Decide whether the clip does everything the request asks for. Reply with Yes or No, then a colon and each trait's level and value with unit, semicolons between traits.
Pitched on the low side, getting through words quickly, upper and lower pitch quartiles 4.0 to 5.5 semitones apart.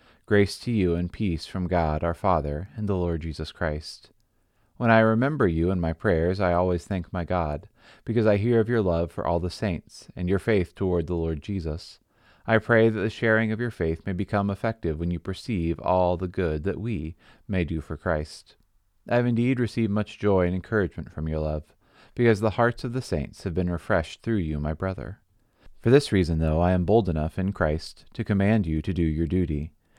Yes: very low, 95 Hz; fast, 215 wpm; average, 4.7 semitones